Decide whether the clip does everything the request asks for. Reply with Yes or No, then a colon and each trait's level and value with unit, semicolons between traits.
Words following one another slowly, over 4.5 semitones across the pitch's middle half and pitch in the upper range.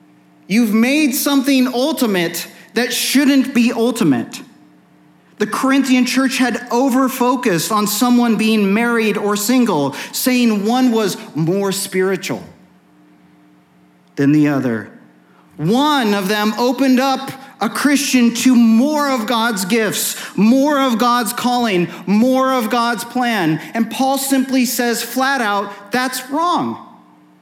Yes: slow, 120 wpm; average, 5.1 semitones; high, 235 Hz